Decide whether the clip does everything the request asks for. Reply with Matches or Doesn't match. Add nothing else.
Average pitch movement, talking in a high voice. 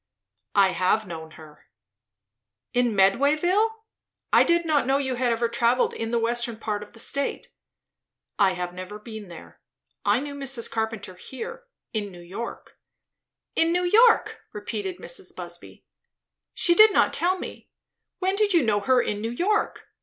Doesn't match